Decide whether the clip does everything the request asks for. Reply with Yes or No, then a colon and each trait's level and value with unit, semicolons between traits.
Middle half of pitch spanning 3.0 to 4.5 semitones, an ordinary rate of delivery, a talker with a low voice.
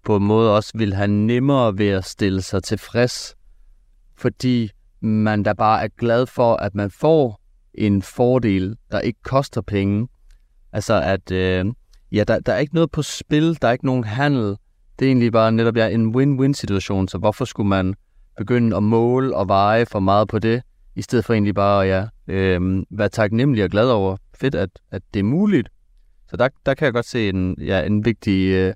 Yes: average, 3.6 semitones; average, 200 wpm; low, 105 Hz